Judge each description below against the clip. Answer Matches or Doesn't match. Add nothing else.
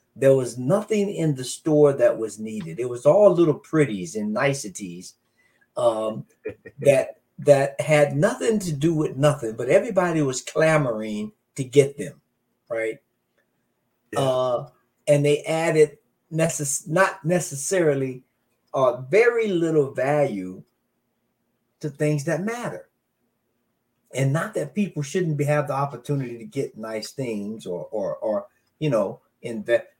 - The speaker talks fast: Doesn't match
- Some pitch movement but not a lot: Matches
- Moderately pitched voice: Matches